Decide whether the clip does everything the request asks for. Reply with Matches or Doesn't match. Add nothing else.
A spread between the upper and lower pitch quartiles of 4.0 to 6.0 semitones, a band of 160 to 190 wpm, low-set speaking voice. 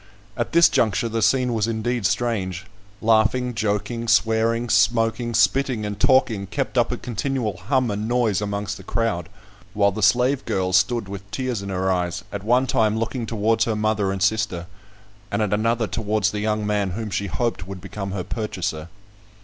Doesn't match